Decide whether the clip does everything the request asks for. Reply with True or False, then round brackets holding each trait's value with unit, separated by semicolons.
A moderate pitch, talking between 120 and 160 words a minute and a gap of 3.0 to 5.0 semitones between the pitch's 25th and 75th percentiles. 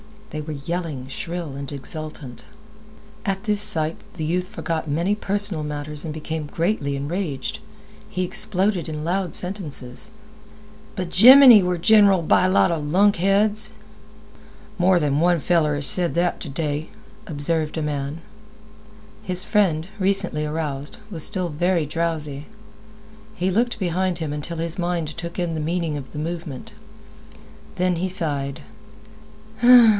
True (170 Hz; 140 wpm; 3.5 semitones)